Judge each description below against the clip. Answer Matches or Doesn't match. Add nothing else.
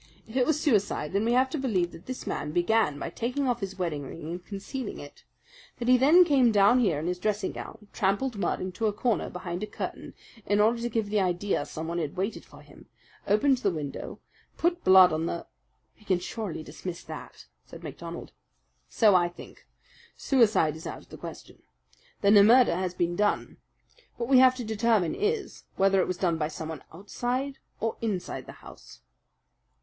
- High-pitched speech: Matches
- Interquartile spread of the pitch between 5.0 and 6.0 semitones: Matches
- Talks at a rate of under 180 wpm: Doesn't match